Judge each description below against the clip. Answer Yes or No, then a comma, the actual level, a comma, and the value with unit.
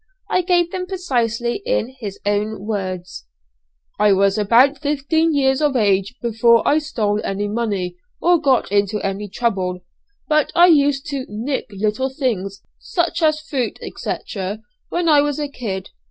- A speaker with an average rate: Yes, average, 155 wpm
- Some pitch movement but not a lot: No, wide, 6.4 semitones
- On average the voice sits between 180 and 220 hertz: No, high, 240 Hz